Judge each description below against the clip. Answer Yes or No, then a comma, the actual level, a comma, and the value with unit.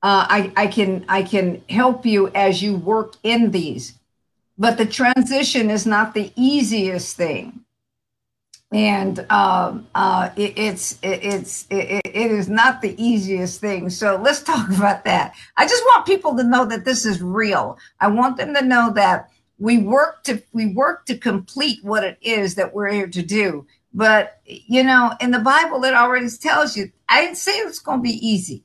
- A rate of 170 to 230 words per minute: Yes, average, 185 wpm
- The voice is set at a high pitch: Yes, high, 215 Hz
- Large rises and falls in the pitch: No, average, 4.2 semitones